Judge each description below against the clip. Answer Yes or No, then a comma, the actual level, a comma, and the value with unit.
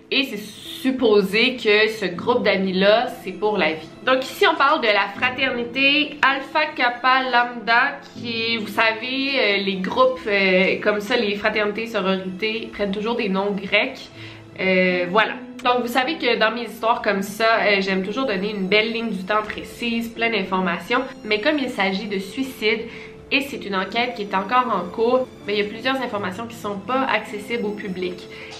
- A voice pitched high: Yes, high, 220 Hz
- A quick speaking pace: No, average, 180 wpm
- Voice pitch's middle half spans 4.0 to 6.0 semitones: No, average, 3.4 semitones